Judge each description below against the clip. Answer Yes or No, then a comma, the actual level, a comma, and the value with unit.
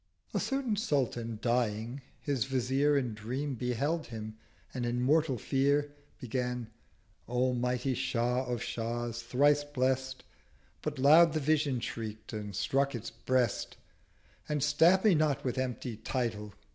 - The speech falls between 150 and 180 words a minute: No, slow, 135 wpm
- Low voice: Yes, low, 130 Hz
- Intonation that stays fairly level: No, average, 3.4 semitones